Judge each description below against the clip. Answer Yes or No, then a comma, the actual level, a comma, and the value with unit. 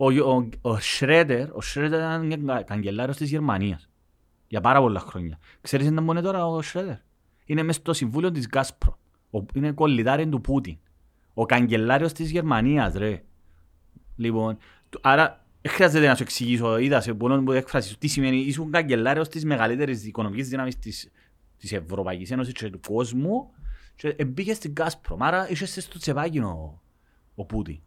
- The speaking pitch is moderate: No, low, 130 Hz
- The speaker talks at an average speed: Yes, average, 145 wpm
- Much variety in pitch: Yes, wide, 7.1 semitones